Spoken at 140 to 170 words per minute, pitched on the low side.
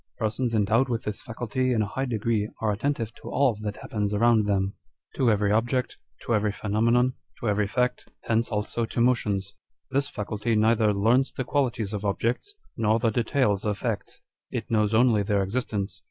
No: average, 185 wpm; low, 110 Hz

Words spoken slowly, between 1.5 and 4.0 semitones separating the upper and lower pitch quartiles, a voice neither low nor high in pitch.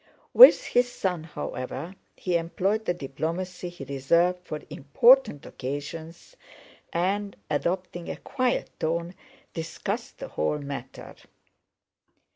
No: slow, 105 wpm; average, 4.4 semitones; medium, 170 Hz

